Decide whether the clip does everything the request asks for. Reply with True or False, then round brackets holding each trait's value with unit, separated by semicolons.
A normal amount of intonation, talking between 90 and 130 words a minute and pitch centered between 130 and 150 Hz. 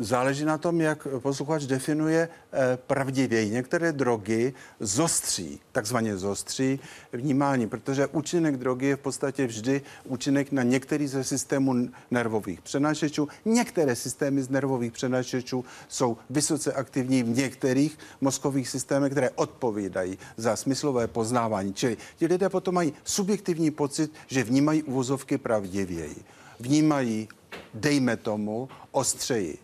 True (3.1 semitones; 120 wpm; 135 Hz)